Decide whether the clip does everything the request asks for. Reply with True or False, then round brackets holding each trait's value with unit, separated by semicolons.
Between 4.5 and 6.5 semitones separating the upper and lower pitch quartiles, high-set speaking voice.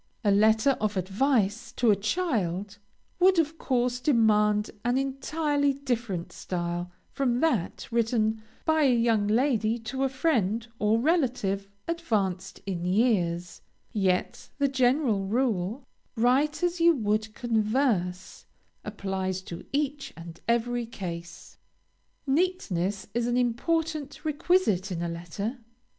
True (5.5 semitones; 230 Hz)